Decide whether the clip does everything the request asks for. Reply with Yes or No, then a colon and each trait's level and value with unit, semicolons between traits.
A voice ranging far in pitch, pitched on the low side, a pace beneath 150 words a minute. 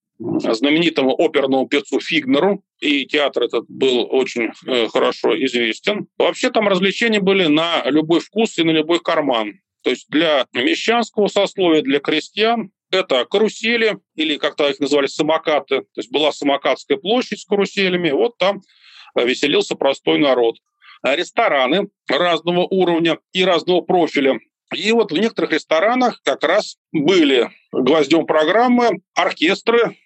No: wide, 7.1 semitones; medium, 185 Hz; average, 130 wpm